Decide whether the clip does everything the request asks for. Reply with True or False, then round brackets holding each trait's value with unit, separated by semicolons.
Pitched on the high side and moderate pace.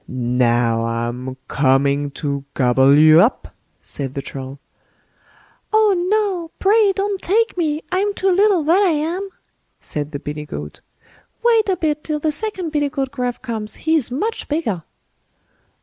True (280 Hz; 150 wpm)